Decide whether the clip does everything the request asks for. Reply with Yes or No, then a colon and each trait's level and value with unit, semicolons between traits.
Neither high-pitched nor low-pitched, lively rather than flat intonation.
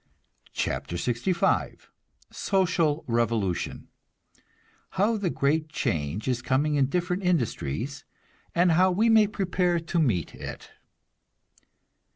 Yes: medium, 155 Hz; wide, 7.2 semitones